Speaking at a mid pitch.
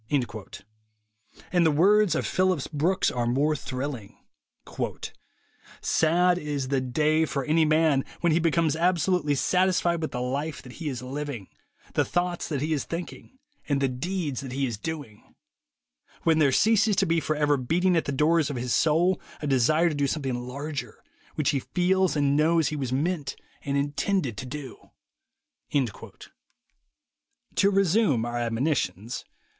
Yes: medium, 150 Hz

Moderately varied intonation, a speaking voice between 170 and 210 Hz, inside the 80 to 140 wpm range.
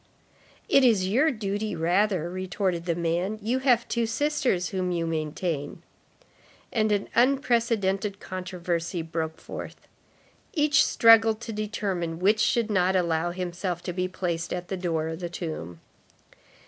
Yes: average, 4.3 semitones; medium, 185 Hz; slow, 135 wpm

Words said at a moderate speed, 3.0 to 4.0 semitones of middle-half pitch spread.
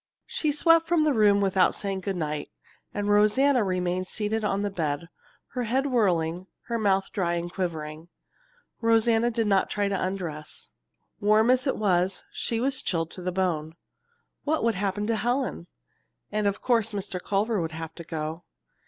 No: average, 170 wpm; average, 4.4 semitones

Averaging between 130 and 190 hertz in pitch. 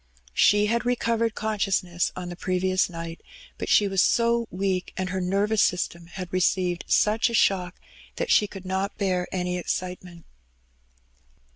Yes: medium, 185 Hz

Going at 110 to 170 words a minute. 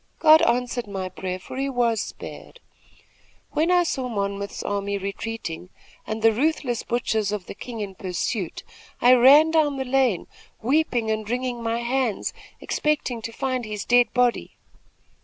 Yes: average, 155 wpm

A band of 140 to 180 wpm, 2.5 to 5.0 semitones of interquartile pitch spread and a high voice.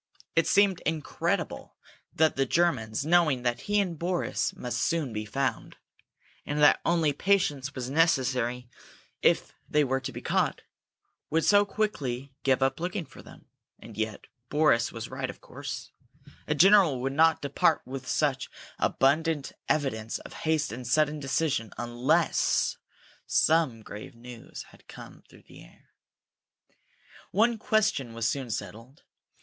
No: average, 145 wpm; average, 4.7 semitones; medium, 140 Hz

